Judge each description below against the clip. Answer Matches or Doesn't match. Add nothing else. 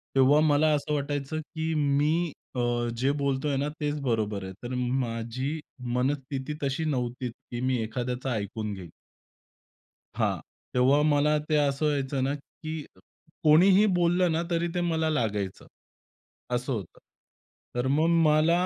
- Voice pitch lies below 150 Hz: Matches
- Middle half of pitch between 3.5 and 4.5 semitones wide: Matches